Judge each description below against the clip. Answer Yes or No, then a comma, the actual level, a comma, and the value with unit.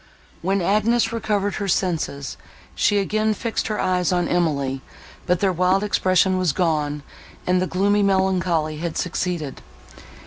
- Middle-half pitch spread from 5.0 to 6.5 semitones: No, average, 3.0 semitones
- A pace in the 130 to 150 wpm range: Yes, average, 140 wpm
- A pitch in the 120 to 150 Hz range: No, medium, 185 Hz